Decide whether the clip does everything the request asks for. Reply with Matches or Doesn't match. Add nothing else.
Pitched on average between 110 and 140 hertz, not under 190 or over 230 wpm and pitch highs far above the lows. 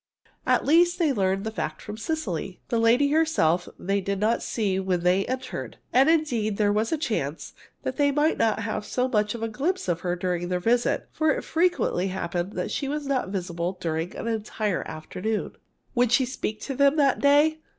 Doesn't match